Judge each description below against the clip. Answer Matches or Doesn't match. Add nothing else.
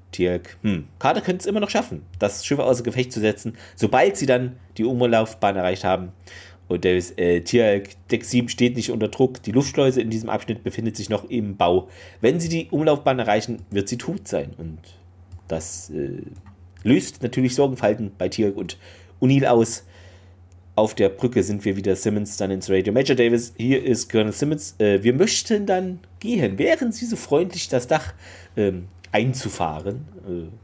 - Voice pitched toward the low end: Matches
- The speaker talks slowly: Doesn't match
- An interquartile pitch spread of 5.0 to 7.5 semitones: Matches